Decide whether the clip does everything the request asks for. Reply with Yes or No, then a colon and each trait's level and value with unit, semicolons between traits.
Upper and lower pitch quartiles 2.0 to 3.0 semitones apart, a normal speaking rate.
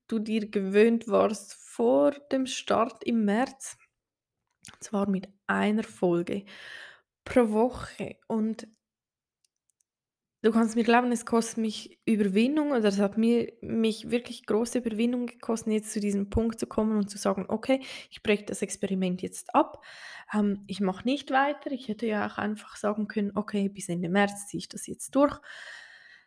Yes: average, 2.7 semitones; average, 160 wpm